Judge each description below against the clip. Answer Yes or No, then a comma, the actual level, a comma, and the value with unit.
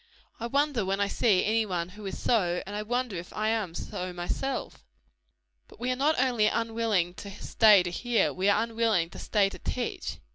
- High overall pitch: Yes, high, 215 Hz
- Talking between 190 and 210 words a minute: Yes, fast, 205 wpm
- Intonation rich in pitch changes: No, average, 3.7 semitones